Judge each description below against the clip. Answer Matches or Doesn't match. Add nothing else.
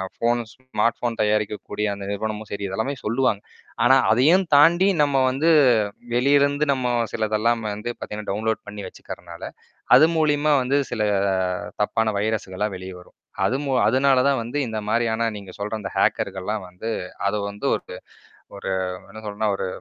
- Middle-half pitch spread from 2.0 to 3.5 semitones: Doesn't match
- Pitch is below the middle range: Matches